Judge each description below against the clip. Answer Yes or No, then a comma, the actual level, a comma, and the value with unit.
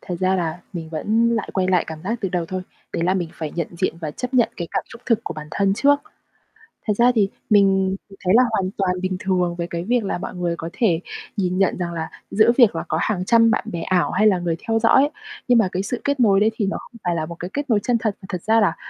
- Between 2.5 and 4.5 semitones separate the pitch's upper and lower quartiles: Yes, average, 4.2 semitones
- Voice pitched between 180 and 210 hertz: Yes, high, 190 Hz